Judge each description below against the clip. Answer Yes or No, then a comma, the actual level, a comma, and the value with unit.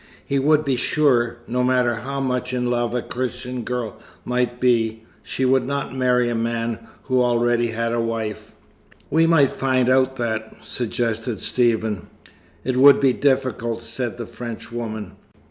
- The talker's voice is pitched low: Yes, low, 125 Hz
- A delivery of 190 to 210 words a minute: No, average, 155 wpm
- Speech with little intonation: Yes, narrow, 1.9 semitones